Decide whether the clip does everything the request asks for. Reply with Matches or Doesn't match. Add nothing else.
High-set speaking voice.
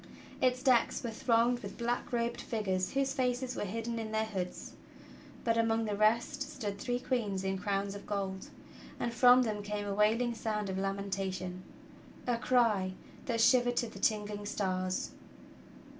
Matches